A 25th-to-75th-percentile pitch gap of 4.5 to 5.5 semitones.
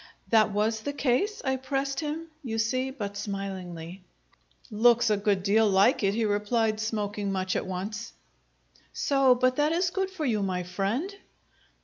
Yes: average, 4.8 semitones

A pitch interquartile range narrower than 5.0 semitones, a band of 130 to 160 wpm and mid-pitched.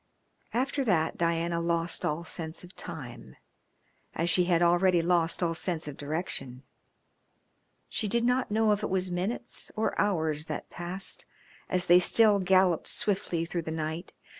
Yes: average, 2.7 semitones; average, 155 wpm; medium, 175 Hz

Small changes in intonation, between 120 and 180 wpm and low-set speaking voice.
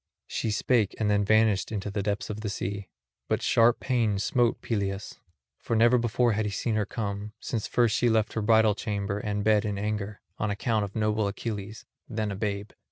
No: narrow, 1.7 semitones; average, 195 wpm; low, 105 Hz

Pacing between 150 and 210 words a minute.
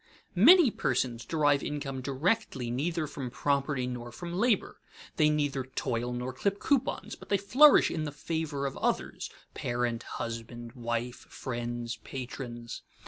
No: average, 140 wpm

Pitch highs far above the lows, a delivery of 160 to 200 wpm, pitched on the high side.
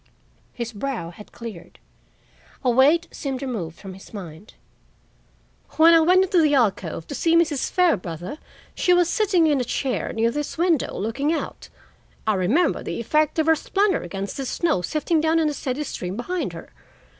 Yes: wide, 7.6 semitones; average, 175 wpm; very high, 275 Hz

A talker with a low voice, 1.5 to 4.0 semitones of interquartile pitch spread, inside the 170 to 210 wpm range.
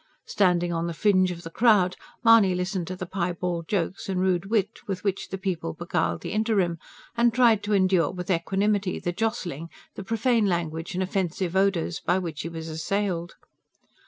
No: medium, 185 Hz; average, 2.8 semitones; average, 180 wpm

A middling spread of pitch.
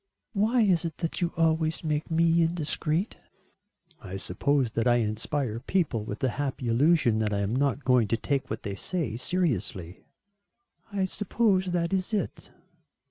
No: wide, 7.0 semitones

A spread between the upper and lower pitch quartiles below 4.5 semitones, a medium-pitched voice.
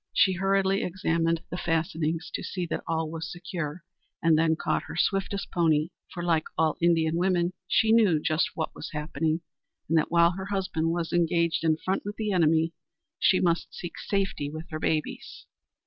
Yes: narrow, 2.4 semitones; medium, 170 Hz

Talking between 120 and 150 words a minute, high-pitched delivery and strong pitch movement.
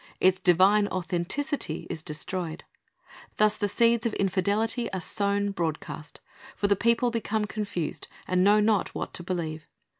No: average, 145 wpm; high, 200 Hz; average, 3.4 semitones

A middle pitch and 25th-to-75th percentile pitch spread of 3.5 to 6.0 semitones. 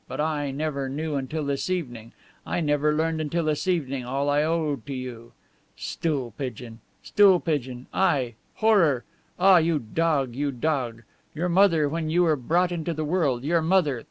Yes: medium, 150 Hz; average, 3.8 semitones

